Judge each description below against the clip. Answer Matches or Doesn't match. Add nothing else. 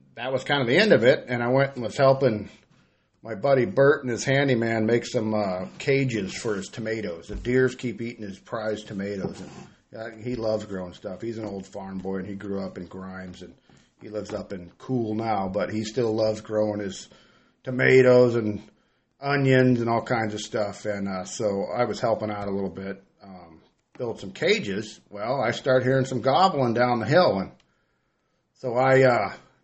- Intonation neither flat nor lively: Matches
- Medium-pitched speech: Doesn't match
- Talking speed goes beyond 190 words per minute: Matches